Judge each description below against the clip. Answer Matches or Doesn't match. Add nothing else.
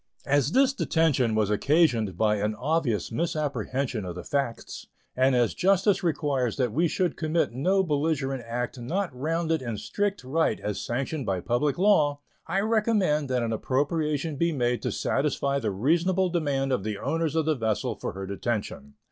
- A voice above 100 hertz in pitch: Matches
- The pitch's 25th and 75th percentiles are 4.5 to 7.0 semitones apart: Matches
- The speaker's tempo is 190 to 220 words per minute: Doesn't match